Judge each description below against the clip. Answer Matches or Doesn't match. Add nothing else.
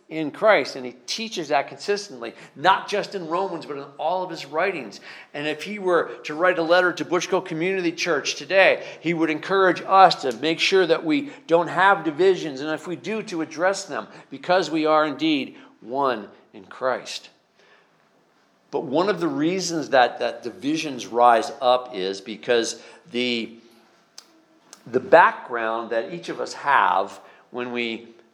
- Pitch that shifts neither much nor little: Doesn't match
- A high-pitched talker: Doesn't match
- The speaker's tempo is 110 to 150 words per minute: Doesn't match